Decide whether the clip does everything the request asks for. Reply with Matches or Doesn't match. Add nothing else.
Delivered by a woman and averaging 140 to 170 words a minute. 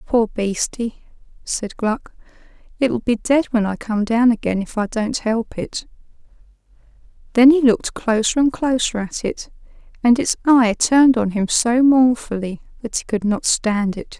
Matches